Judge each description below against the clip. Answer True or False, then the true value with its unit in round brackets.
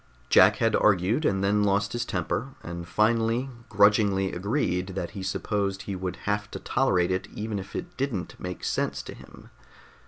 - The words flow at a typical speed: True (175 wpm)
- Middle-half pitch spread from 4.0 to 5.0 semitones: False (2.7 semitones)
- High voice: False (100 Hz)